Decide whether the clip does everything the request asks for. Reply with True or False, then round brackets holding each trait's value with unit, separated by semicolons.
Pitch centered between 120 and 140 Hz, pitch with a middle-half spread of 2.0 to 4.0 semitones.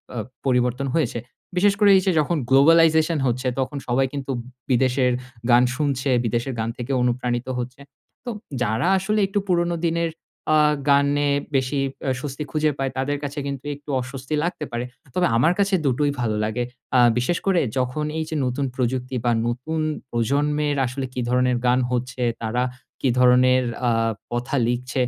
True (135 Hz; 3.4 semitones)